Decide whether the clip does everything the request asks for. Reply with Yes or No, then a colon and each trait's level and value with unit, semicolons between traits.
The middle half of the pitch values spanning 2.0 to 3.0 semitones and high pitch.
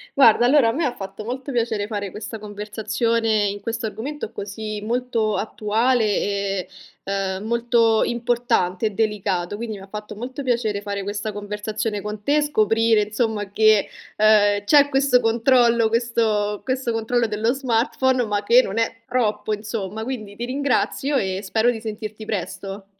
Yes: narrow, 2.6 semitones; high, 220 Hz